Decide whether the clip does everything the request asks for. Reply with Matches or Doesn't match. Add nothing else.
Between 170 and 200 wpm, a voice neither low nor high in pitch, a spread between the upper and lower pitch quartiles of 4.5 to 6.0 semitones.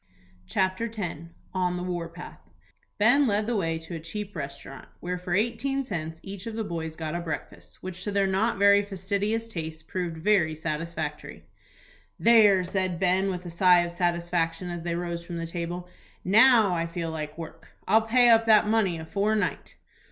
Doesn't match